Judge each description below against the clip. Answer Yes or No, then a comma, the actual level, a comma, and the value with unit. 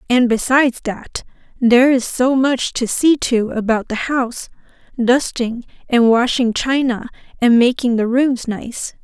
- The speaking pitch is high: Yes, high, 245 Hz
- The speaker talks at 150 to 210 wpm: No, average, 140 wpm